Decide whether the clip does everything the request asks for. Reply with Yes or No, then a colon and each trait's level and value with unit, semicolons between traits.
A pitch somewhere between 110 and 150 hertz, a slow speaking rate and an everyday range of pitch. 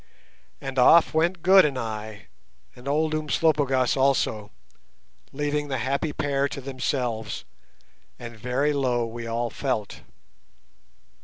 Yes: low, 135 Hz; slow, 120 wpm; average, 3.7 semitones